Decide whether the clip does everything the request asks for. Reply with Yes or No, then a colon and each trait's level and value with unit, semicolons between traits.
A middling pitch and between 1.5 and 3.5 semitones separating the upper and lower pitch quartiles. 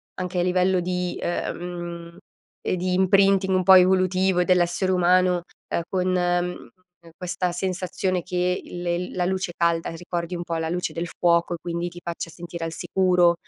No: medium, 180 Hz; narrow, 1.1 semitones